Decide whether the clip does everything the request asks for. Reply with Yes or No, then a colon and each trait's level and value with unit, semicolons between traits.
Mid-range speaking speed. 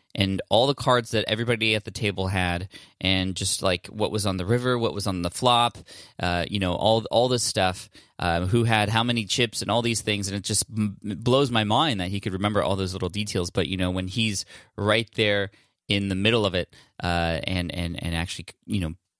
No: fast, 230 wpm